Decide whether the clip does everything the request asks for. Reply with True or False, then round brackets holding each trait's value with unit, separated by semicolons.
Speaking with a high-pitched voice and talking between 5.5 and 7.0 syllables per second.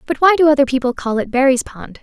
True (270 Hz; 6.5 syllables/s)